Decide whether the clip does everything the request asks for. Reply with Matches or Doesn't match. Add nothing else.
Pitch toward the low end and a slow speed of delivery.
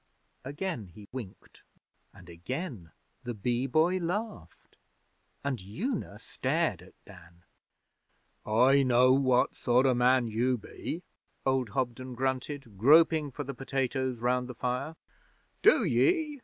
Matches